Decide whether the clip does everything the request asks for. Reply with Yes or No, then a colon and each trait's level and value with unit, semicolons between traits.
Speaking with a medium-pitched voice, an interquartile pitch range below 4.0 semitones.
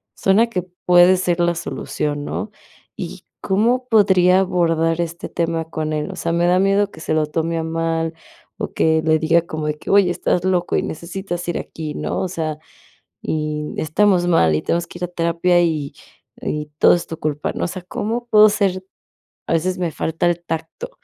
Yes: medium, 170 Hz; narrow, 2.5 semitones